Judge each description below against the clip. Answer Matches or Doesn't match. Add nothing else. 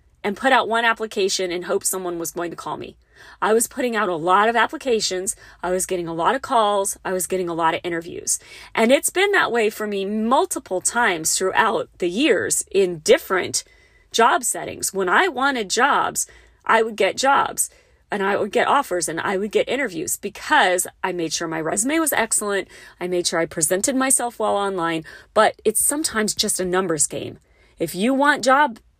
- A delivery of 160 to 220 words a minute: Matches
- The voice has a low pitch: Doesn't match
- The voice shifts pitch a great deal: Matches